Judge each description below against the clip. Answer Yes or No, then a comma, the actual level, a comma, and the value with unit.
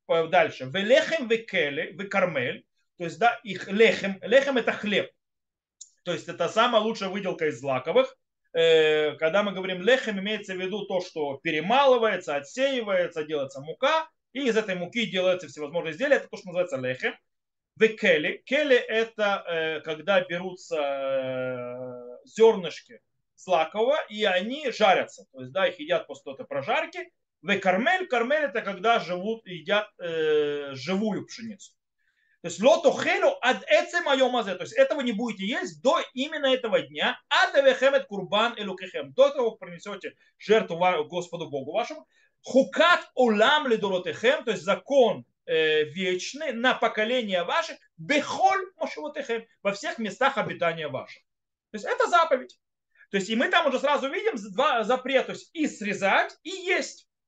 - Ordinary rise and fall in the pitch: No, wide, 7.1 semitones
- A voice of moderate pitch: No, high, 220 Hz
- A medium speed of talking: Yes, average, 145 wpm